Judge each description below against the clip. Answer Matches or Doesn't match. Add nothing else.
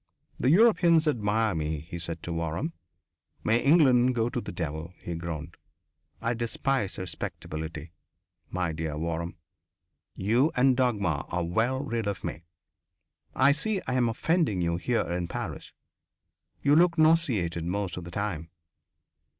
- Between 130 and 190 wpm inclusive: Matches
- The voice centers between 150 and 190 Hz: Doesn't match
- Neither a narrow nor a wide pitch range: Doesn't match